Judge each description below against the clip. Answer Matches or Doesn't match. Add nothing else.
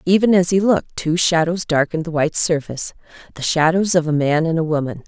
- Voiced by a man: Doesn't match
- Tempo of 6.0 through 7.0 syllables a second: Matches